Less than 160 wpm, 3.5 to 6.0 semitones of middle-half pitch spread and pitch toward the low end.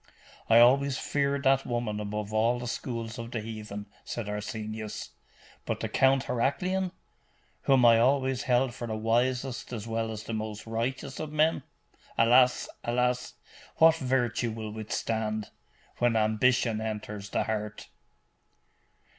No: average, 140 wpm; average, 3.1 semitones; low, 115 Hz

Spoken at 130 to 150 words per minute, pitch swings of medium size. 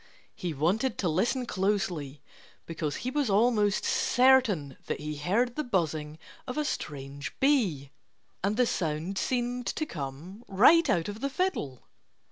No: average, 145 wpm; wide, 8.5 semitones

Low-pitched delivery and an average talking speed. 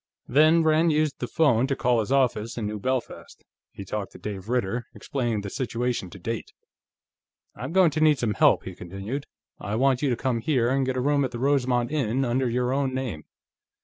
No: low, 125 Hz; fast, 210 wpm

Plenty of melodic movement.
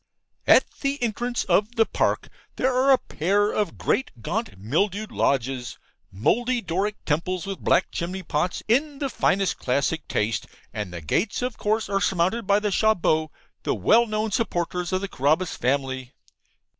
Yes: wide, 6.1 semitones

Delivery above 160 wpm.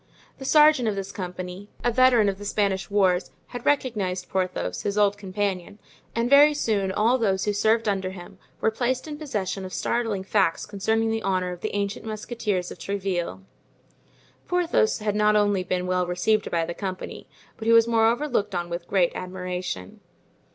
Yes: average, 180 wpm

